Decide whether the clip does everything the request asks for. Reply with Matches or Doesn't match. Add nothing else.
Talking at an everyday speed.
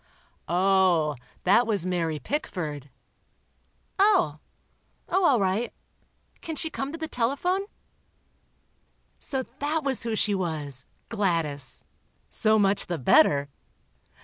Doesn't match